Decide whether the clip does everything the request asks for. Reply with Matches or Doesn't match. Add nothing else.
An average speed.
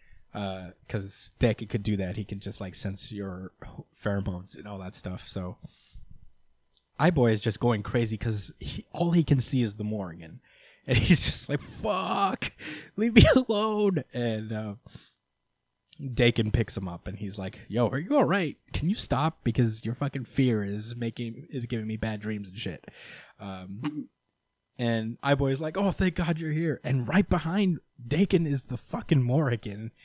Matches